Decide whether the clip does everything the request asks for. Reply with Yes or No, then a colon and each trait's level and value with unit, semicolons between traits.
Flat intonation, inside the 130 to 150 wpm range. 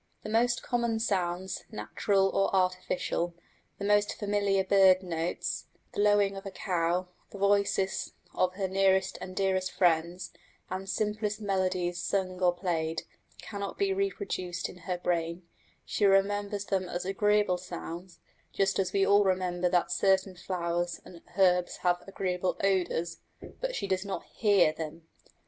Yes: narrow, 2.1 semitones; average, 145 wpm